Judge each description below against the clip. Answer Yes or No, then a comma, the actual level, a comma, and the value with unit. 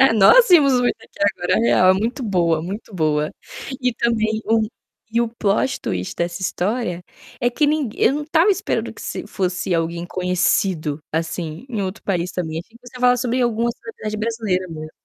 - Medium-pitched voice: No, high, 210 Hz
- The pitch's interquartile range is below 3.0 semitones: No, wide, 5.6 semitones